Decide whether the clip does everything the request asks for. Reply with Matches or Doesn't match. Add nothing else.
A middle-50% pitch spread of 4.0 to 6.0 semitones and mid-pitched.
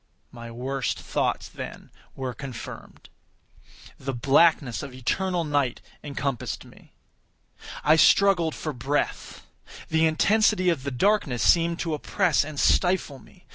Matches